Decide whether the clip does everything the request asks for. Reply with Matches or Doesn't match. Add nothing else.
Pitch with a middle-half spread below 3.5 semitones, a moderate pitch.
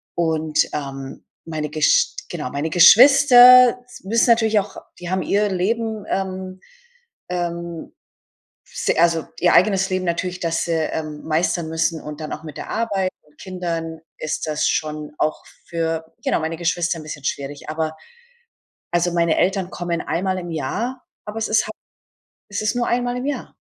Doesn't match